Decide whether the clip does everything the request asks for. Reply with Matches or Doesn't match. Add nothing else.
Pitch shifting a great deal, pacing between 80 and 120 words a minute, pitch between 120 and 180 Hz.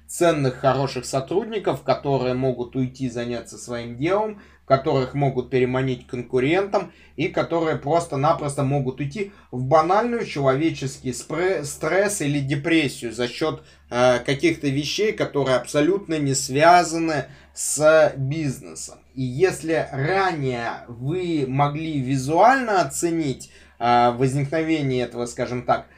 Doesn't match